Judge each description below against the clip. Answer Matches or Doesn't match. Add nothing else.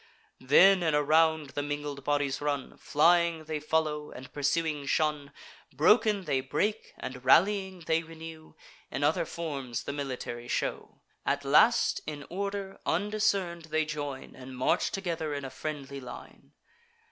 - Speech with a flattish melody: Doesn't match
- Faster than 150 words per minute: Doesn't match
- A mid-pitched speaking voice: Matches